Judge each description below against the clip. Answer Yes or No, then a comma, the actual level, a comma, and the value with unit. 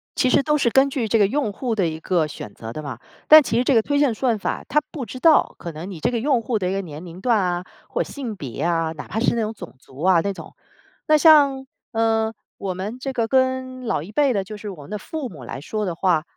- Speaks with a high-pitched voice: Yes, high, 220 Hz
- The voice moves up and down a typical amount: No, wide, 6.6 semitones